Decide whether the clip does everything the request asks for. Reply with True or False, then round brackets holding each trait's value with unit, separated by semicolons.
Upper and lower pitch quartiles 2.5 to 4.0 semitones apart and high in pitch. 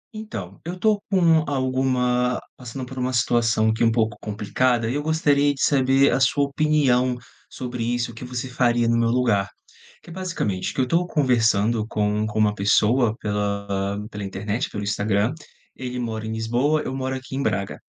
False (3.6 semitones; 125 Hz)